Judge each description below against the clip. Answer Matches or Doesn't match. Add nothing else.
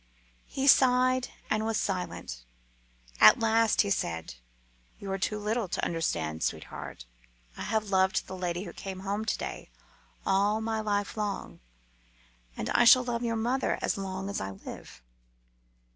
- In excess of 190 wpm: Doesn't match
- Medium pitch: Doesn't match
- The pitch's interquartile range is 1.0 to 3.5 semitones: Matches